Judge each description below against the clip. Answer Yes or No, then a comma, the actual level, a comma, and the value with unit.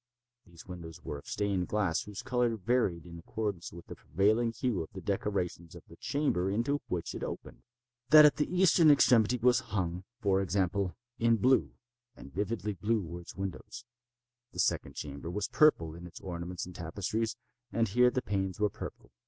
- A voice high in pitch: No, low, 100 Hz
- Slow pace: No, average, 175 wpm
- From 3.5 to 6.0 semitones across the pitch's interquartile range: Yes, average, 5.1 semitones